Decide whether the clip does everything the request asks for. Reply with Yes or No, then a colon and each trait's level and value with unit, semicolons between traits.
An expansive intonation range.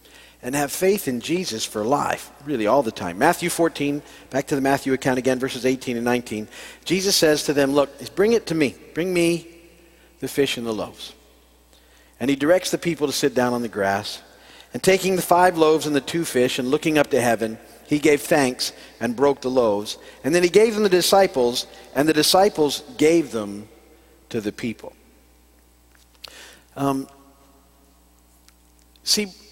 Yes: wide, 6.7 semitones